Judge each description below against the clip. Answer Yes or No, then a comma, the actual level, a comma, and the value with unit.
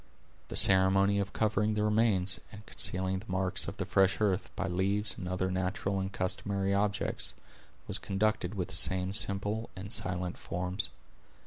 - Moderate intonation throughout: No, narrow, 1.7 semitones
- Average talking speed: Yes, average, 160 wpm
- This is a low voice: Yes, very low, 95 Hz